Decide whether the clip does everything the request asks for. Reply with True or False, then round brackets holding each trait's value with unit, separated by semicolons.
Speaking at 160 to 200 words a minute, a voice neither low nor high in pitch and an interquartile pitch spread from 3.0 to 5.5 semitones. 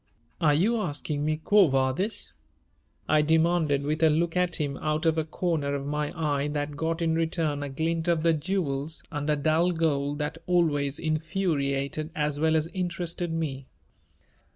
False (165 wpm; 155 Hz; 2.4 semitones)